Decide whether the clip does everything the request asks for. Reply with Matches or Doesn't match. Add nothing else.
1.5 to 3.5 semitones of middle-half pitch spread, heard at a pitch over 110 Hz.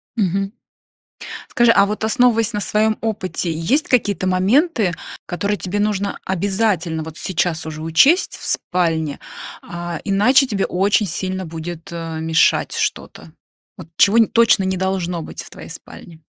Doesn't match